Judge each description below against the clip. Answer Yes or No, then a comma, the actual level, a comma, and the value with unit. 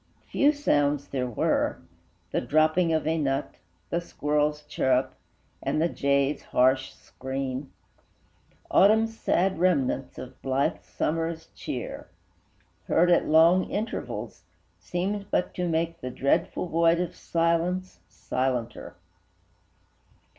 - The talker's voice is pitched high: No, medium, 160 Hz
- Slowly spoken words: Yes, slow, 110 wpm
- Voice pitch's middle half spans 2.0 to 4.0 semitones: No, average, 4.4 semitones